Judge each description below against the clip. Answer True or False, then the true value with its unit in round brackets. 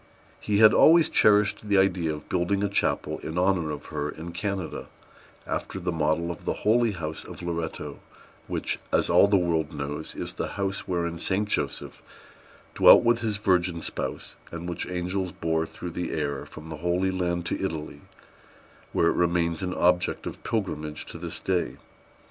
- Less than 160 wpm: False (175 wpm)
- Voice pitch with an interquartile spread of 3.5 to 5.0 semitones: False (3.1 semitones)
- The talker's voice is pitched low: True (85 Hz)